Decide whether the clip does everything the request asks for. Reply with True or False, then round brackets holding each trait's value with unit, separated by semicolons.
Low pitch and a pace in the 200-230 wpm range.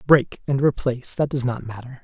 True (130 Hz; 205 wpm)